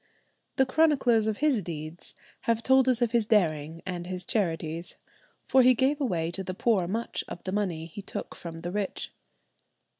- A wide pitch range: Yes, wide, 5.9 semitones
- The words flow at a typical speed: Yes, average, 180 wpm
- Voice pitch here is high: Yes, high, 200 Hz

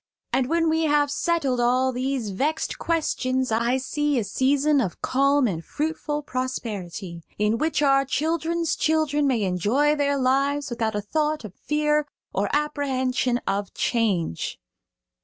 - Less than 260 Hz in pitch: No, very high, 270 Hz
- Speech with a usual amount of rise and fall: Yes, average, 4.0 semitones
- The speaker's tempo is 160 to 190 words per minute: No, average, 140 wpm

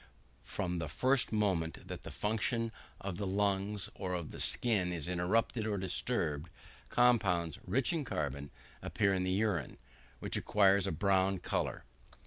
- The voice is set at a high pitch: No, very low, 95 Hz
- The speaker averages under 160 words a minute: Yes, average, 150 wpm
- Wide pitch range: No, average, 3.3 semitones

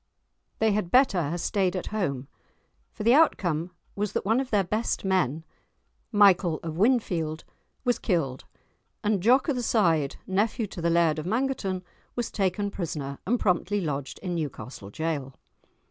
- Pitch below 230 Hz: Yes, medium, 185 Hz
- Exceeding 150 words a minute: Yes, average, 160 wpm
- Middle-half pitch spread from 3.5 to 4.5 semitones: No, average, 5.0 semitones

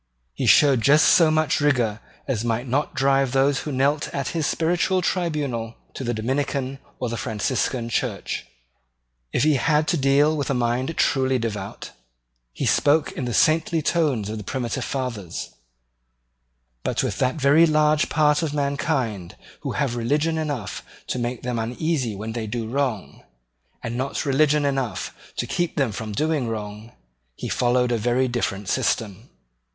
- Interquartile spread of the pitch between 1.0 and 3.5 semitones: No, average, 4.2 semitones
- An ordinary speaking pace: Yes, average, 160 wpm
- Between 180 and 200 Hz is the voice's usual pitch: No, low, 130 Hz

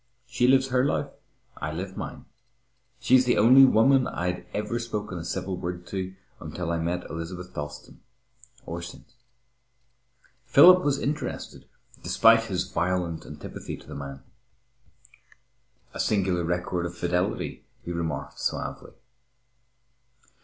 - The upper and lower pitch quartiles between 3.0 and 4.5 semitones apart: No, wide, 5.4 semitones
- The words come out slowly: Yes, slow, 125 wpm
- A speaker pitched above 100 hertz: No, very low, 90 Hz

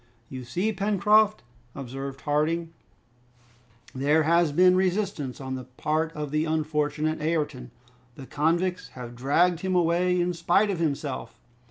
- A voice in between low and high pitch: Yes, medium, 155 Hz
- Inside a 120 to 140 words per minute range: Yes, slow, 135 wpm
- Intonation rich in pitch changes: No, average, 4.2 semitones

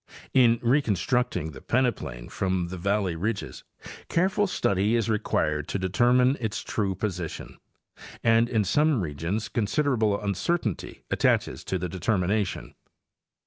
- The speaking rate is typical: No, slow, 125 wpm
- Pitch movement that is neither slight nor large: Yes, average, 4.8 semitones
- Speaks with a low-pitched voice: Yes, low, 105 Hz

